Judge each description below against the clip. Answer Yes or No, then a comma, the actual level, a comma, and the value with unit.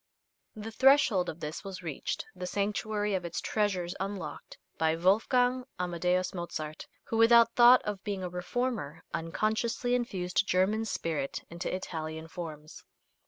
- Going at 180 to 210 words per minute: No, slow, 135 wpm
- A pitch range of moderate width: Yes, average, 4.5 semitones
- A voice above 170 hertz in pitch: Yes, medium, 185 Hz